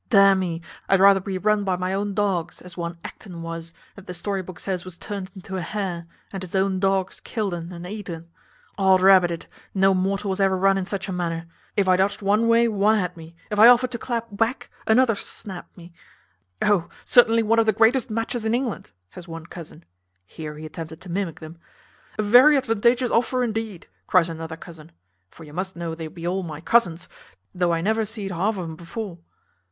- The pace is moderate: No, fast, 215 wpm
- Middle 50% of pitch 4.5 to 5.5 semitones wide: No, average, 3.7 semitones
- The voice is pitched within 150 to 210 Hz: Yes, high, 190 Hz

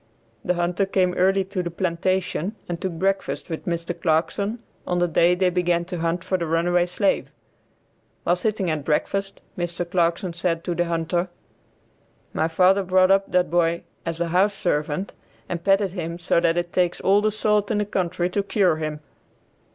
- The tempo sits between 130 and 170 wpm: No, average, 180 wpm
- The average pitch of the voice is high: No, medium, 175 Hz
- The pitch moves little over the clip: Yes, narrow, 2.2 semitones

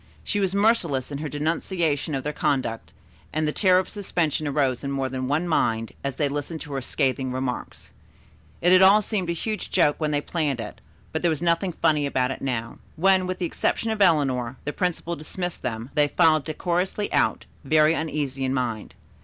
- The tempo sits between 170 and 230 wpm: Yes, average, 200 wpm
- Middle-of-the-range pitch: Yes, medium, 150 Hz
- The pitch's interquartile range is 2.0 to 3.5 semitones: No, average, 4.6 semitones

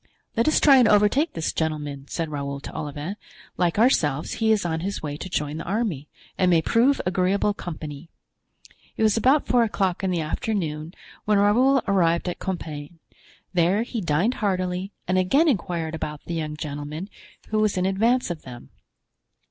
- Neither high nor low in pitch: Yes, medium, 180 Hz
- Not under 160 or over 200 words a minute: Yes, average, 175 wpm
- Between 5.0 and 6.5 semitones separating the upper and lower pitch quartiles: Yes, wide, 5.4 semitones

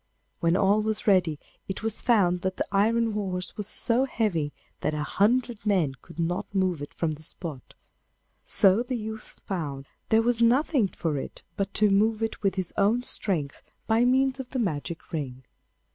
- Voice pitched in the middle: No, high, 200 Hz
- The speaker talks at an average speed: Yes, average, 180 wpm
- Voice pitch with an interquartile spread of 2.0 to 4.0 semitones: No, average, 5.0 semitones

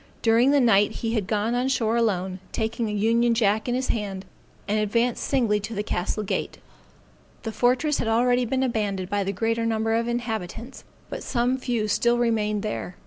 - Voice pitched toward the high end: Yes, high, 225 Hz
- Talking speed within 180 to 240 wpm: Yes, average, 195 wpm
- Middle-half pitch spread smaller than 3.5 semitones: Yes, narrow, 2.4 semitones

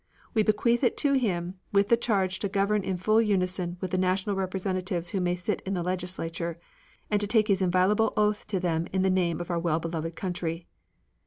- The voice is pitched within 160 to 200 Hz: Yes, medium, 185 Hz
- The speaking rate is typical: No, fast, 210 wpm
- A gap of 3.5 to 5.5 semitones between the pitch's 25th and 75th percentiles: No, average, 2.7 semitones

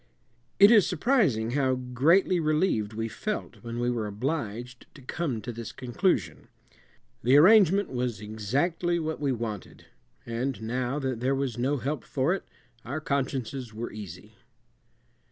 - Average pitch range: Yes, average, 4.9 semitones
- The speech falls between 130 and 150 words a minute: Yes, average, 145 wpm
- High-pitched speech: No, low, 130 Hz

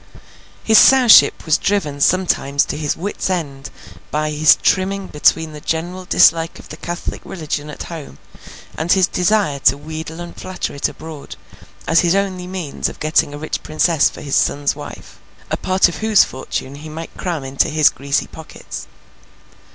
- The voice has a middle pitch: Yes, medium, 160 Hz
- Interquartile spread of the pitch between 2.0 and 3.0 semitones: No, average, 3.7 semitones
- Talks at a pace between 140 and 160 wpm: No, average, 170 wpm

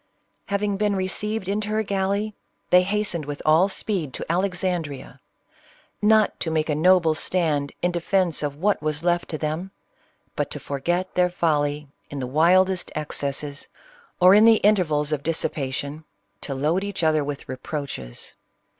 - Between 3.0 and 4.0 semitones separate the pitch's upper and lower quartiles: No, average, 4.4 semitones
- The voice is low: No, medium, 170 Hz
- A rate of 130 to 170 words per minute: Yes, average, 160 wpm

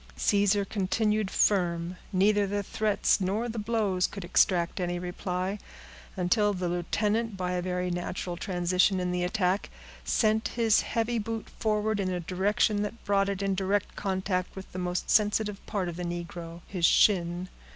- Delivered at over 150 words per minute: Yes, average, 160 wpm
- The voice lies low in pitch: No, high, 190 Hz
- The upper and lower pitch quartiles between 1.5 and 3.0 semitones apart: Yes, average, 2.7 semitones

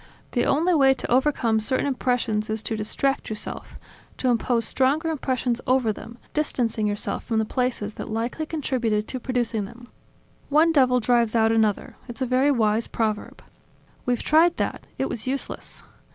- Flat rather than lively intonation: No, average, 3.3 semitones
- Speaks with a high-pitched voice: Yes, high, 245 Hz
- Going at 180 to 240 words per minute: No, average, 165 wpm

